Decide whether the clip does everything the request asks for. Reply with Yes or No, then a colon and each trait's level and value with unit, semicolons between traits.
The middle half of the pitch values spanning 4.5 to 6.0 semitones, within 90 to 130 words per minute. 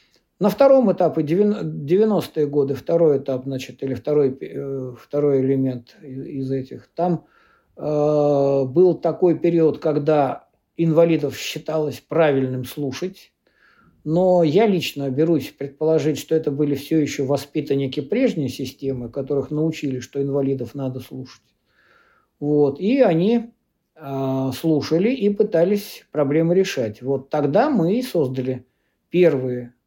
No: average, 3.7 semitones; average, 115 wpm